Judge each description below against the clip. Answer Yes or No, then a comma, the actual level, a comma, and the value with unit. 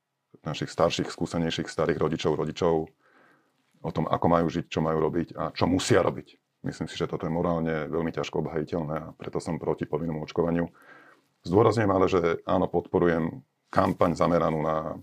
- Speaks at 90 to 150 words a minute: No, fast, 165 wpm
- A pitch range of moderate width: No, narrow, 1.3 semitones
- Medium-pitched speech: No, very low, 80 Hz